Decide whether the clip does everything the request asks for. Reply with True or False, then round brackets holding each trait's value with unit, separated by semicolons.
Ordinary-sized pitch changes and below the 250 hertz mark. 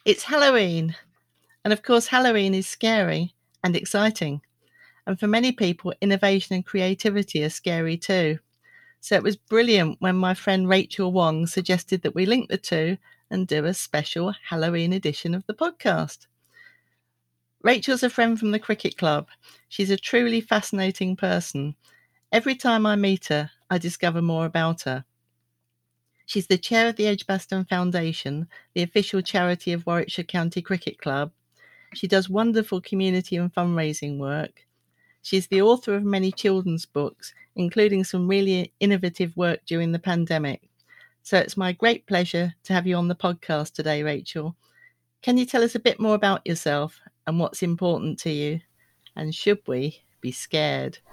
True (3.9 semitones; 185 Hz)